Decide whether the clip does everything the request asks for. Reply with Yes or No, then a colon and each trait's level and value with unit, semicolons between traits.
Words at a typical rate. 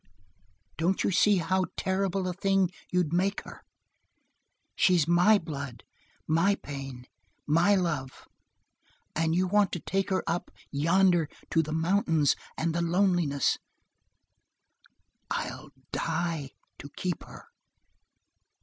No: slow, 115 wpm